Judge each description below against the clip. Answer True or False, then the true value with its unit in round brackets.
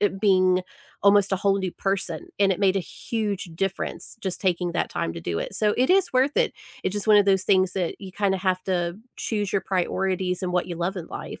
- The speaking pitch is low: False (190 Hz)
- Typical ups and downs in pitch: False (1.9 semitones)